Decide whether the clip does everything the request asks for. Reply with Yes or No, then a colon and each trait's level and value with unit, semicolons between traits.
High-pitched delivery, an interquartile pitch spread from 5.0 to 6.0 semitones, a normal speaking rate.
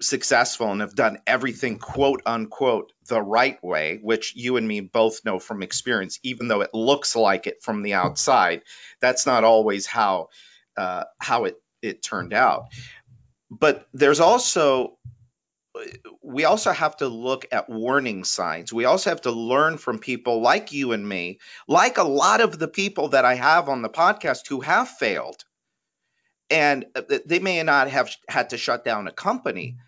No: low, 125 Hz; wide, 5.6 semitones; average, 170 wpm